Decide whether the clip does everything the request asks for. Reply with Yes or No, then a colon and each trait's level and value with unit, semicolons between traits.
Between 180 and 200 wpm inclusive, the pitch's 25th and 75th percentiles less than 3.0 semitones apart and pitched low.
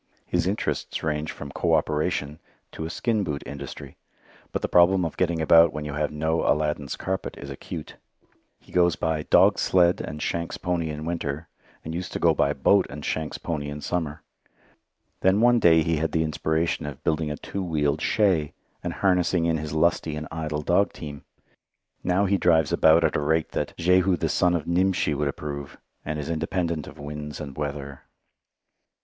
Yes: average, 185 wpm; narrow, 2.6 semitones; very low, 80 Hz